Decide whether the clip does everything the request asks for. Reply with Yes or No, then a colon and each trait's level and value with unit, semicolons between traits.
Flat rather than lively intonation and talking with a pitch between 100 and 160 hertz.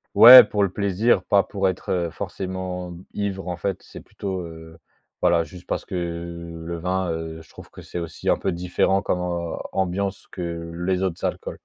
No: narrow, 2.1 semitones; very low, 90 Hz